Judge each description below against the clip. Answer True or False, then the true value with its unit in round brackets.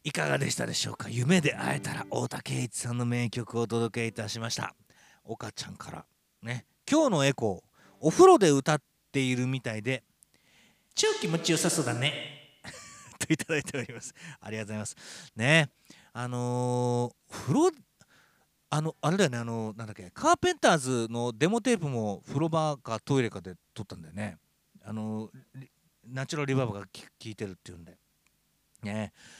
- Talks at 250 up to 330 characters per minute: False (345 characters per minute)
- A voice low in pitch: True (125 Hz)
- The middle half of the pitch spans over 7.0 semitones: False (5.5 semitones)